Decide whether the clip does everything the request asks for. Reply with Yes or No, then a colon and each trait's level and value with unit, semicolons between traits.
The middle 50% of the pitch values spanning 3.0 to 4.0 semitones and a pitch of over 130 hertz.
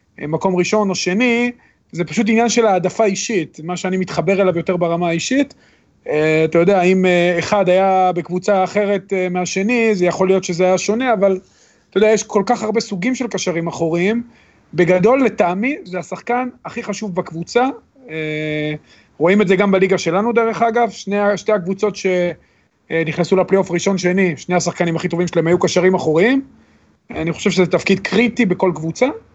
Yes: average, 3.4 semitones; high, 190 Hz